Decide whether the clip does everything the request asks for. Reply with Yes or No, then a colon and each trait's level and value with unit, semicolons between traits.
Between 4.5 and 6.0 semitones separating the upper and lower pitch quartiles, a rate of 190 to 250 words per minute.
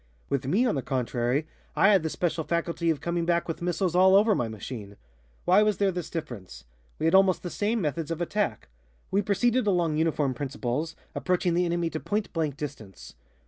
Yes: average, 4.8 semitones; average, 195 wpm